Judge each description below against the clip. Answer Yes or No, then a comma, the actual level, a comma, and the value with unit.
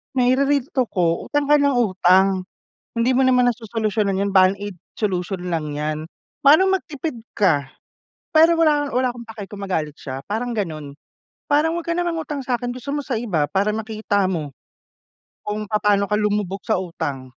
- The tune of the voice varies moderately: No, wide, 5.7 semitones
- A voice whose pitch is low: No, high, 215 Hz